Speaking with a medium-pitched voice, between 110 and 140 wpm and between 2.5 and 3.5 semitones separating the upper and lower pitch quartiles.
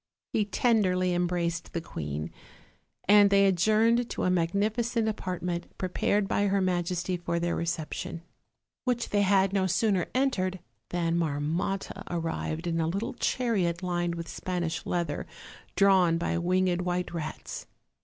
Yes: medium, 180 Hz; slow, 135 wpm; average, 2.8 semitones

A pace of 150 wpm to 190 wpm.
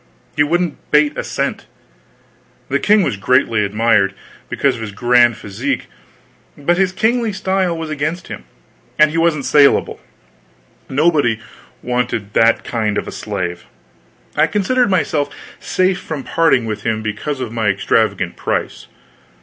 No: average, 140 wpm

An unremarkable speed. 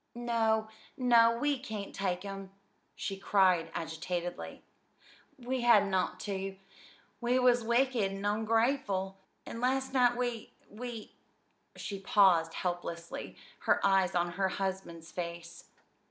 No: slow, 125 wpm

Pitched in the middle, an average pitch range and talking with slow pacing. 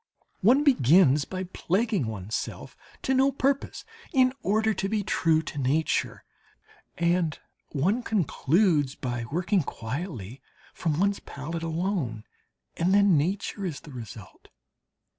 No: medium, 170 Hz; wide, 6.2 semitones; slow, 125 wpm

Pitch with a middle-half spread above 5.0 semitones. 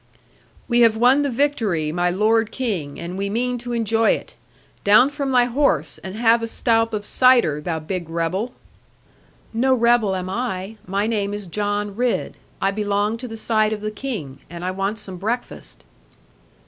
No: average, 3.9 semitones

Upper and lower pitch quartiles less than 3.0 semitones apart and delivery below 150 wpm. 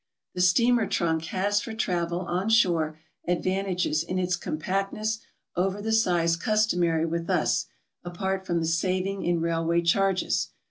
Yes: narrow, 2.6 semitones; average, 140 wpm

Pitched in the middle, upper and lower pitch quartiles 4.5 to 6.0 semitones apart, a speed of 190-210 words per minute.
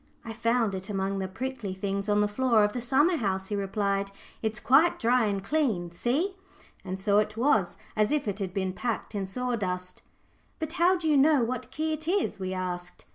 No: high, 215 Hz; average, 5.2 semitones; fast, 205 wpm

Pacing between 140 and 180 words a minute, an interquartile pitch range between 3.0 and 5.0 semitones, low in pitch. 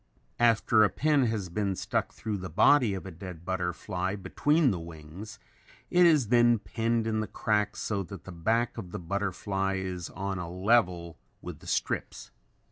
Yes: average, 175 wpm; average, 4.0 semitones; low, 100 Hz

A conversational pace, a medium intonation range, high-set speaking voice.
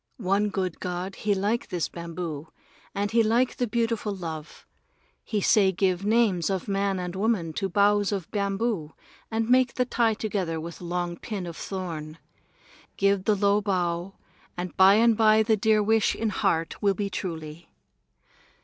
Yes: average, 165 wpm; average, 3.5 semitones; high, 195 Hz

